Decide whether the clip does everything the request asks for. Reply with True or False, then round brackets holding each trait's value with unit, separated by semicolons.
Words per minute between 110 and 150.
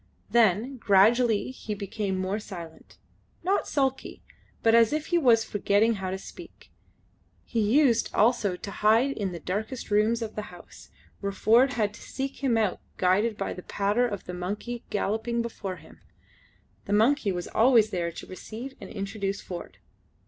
False (165 wpm)